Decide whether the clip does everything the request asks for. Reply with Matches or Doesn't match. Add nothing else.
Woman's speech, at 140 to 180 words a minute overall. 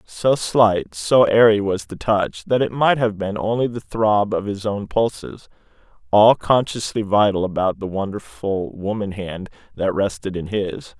Doesn't match